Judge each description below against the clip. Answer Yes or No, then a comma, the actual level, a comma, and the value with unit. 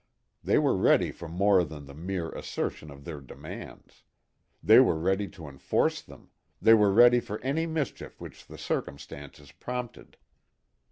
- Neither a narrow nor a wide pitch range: No, wide, 7.4 semitones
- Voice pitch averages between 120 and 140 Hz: No, very low, 95 Hz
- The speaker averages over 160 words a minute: No, average, 155 wpm